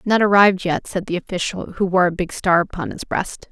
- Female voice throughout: Yes, female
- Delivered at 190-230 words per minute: No, fast, 240 wpm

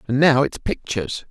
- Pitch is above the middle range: No, low, 120 Hz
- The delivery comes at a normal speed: Yes, average, 185 wpm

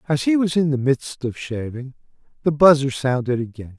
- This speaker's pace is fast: No, average, 190 wpm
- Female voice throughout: No, male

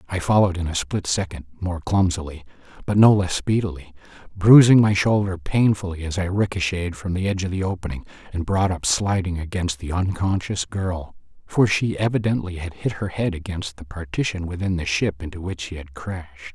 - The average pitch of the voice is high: No, very low, 90 Hz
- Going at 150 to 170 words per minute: No, average, 185 wpm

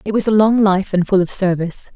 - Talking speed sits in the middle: No, fast, 275 wpm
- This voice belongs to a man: No, female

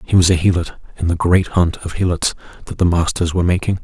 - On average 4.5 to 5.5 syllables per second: No, 6.3 syllables/s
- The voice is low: Yes, very low, 85 Hz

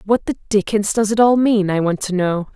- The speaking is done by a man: No, female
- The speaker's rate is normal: No, fast, 260 wpm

